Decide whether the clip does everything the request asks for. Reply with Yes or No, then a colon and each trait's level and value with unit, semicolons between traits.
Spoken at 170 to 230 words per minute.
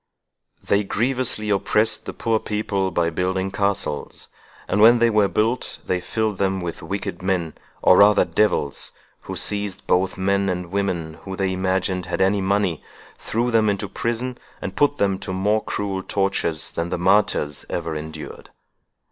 No: average, 160 wpm